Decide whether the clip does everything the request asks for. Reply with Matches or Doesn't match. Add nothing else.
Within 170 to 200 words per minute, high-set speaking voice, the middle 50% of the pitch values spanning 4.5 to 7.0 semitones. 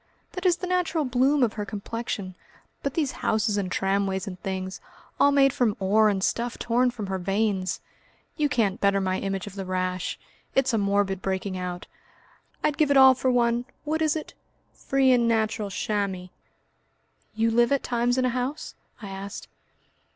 Matches